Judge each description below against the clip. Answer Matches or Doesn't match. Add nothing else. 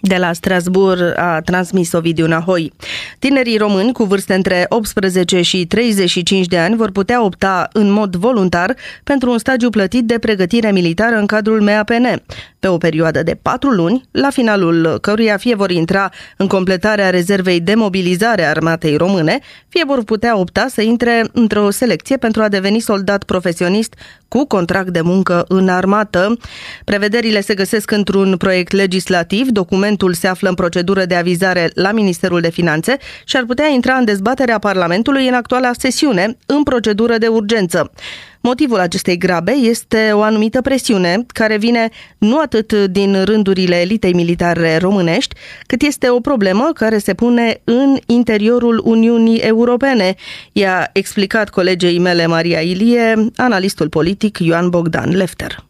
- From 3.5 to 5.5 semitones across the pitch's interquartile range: Matches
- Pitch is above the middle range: Matches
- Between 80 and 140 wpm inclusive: Doesn't match